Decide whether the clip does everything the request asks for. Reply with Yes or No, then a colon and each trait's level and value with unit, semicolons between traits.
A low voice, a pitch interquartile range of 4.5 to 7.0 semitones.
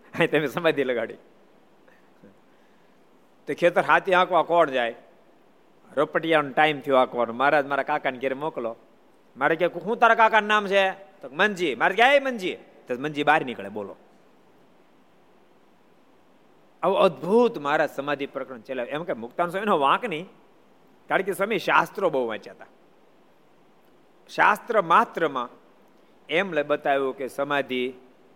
No: medium, 150 Hz; wide, 5.6 semitones